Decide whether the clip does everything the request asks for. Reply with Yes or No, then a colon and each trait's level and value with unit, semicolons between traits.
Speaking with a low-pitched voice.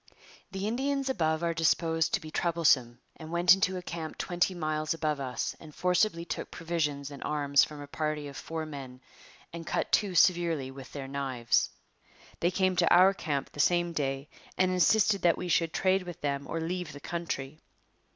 No: medium, 165 Hz